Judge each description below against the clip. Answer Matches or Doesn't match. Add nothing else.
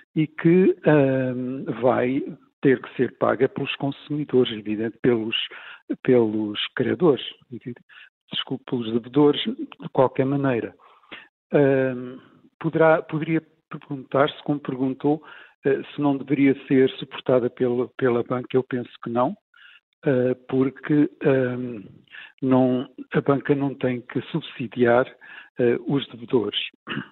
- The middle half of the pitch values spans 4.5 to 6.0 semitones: Doesn't match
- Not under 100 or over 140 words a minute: Matches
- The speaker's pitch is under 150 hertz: Matches